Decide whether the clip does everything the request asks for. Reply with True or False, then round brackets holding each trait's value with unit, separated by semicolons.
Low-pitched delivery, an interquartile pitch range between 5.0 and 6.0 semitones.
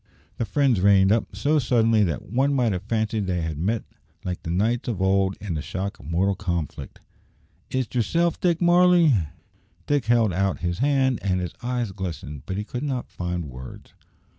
True (105 Hz; 5.6 semitones)